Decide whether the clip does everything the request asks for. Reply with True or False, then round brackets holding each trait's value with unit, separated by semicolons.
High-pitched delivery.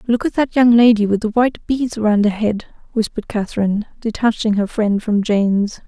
True (220 Hz)